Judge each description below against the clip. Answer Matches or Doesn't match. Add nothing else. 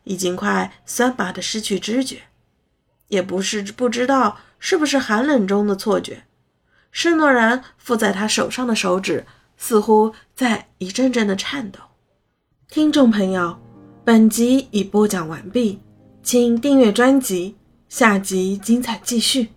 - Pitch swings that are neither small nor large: Matches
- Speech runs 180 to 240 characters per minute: Matches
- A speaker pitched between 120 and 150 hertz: Doesn't match